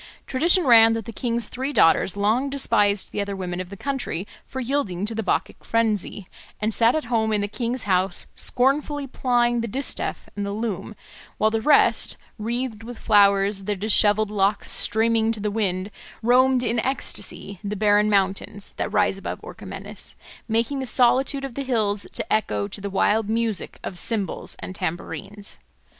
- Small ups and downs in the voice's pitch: No, average, 3.2 semitones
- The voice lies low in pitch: No, high, 220 Hz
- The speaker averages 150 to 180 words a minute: Yes, average, 175 wpm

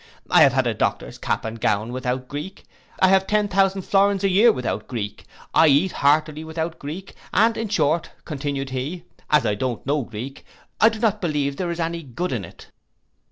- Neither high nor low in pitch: Yes, medium, 155 Hz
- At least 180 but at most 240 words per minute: Yes, average, 200 wpm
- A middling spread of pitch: No, wide, 6.3 semitones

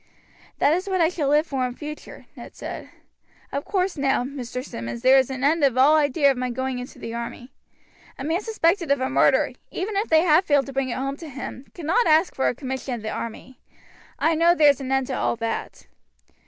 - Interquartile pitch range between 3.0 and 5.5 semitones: Yes, average, 3.9 semitones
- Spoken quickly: Yes, fast, 225 wpm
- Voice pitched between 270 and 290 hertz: Yes, very high, 280 Hz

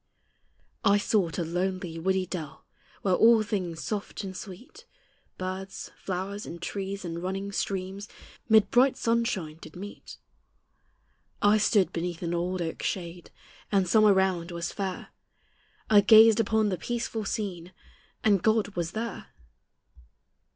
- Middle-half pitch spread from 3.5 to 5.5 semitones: No, average, 3.1 semitones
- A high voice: Yes, high, 195 Hz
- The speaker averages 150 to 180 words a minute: No, slow, 135 wpm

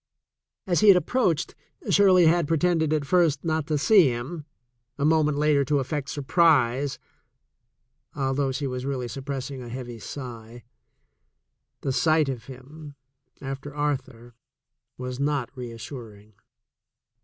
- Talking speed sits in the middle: No, slow, 125 wpm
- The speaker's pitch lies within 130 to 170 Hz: Yes, medium, 140 Hz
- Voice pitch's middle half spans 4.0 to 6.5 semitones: No, average, 3.6 semitones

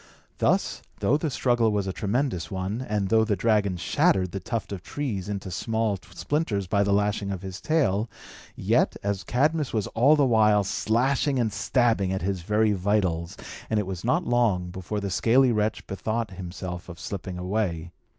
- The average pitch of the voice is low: Yes, low, 105 Hz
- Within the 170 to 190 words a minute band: Yes, average, 175 wpm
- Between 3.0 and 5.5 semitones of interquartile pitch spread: Yes, average, 3.6 semitones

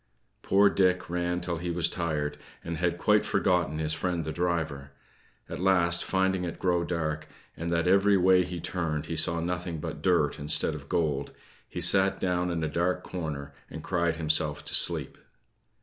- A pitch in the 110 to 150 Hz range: No, very low, 85 Hz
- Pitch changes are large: No, narrow, 2.4 semitones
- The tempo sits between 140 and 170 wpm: No, average, 180 wpm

